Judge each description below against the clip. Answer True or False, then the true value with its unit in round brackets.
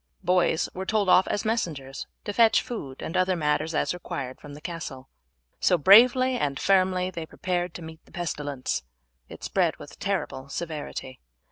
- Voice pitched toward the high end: False (170 Hz)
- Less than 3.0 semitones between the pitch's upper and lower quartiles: False (4.4 semitones)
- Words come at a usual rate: True (165 wpm)